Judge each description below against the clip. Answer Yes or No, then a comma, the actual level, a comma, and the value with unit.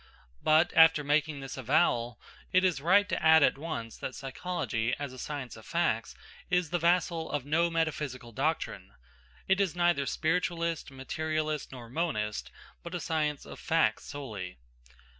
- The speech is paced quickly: No, average, 155 wpm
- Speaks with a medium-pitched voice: Yes, medium, 155 Hz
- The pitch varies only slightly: No, average, 4.1 semitones